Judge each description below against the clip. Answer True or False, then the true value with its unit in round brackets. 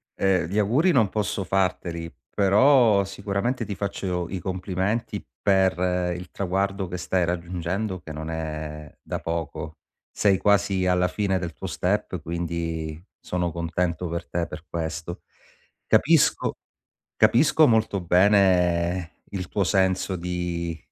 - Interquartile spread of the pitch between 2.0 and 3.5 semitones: True (2.6 semitones)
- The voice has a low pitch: True (90 Hz)